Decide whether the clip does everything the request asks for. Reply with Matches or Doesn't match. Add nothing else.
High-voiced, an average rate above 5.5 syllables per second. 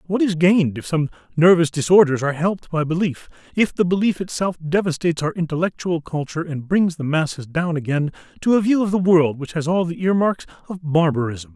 Doesn't match